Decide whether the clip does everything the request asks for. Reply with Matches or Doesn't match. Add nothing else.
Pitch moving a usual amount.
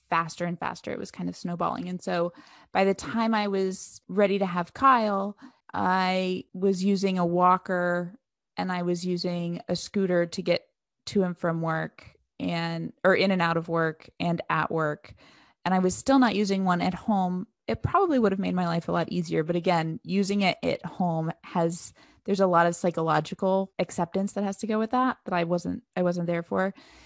Doesn't match